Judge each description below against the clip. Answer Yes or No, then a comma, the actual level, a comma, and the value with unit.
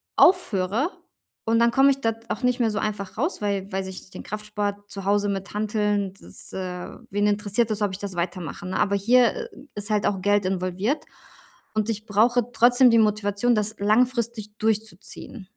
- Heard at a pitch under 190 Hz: No, high, 210 Hz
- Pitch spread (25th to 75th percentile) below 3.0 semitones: Yes, narrow, 2.5 semitones